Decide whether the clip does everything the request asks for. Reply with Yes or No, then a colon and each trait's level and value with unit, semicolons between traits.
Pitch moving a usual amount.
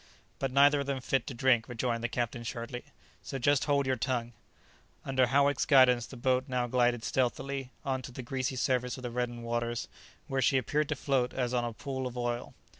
No: narrow, 1.9 semitones